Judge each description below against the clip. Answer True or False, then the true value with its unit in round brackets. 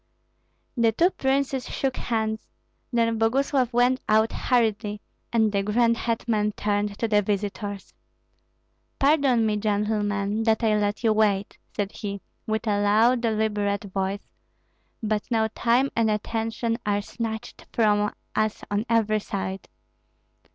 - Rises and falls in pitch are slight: True (2.0 semitones)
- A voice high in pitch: True (220 Hz)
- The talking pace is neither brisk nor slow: False (130 wpm)